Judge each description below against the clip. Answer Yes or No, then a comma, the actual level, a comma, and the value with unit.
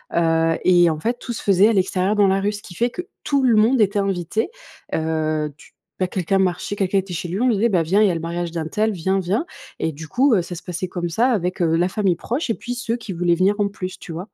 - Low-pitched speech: No, high, 190 Hz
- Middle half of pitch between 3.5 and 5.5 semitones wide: Yes, average, 3.8 semitones